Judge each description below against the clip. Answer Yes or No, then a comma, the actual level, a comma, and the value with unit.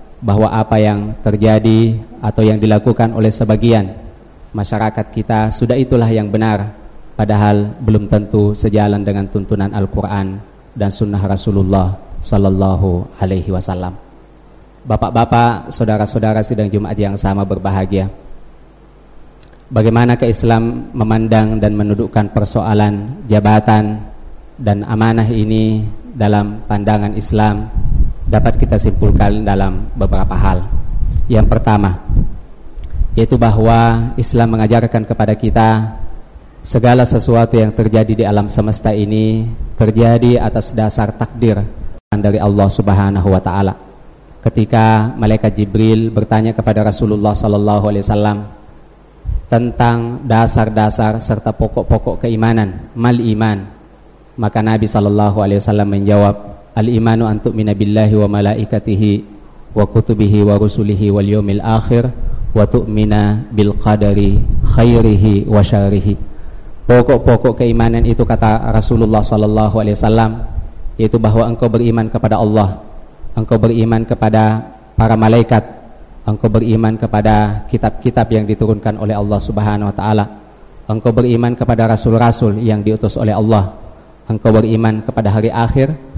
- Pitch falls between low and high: No, low, 110 Hz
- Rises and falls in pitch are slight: Yes, narrow, 1.6 semitones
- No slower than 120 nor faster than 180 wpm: No, average, 110 wpm